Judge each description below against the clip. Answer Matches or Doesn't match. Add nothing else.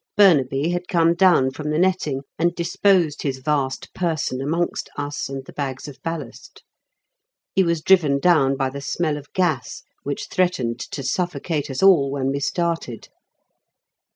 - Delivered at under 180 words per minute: Matches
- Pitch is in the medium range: Matches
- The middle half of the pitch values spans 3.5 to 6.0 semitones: Matches